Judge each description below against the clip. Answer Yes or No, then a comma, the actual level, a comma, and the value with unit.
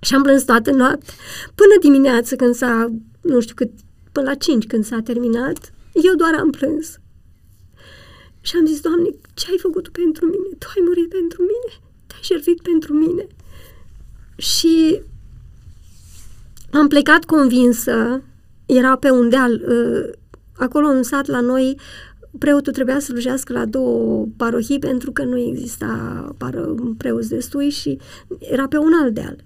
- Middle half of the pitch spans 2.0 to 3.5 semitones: No, wide, 5.4 semitones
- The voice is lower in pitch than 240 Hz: No, very high, 265 Hz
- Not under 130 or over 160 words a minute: Yes, average, 150 wpm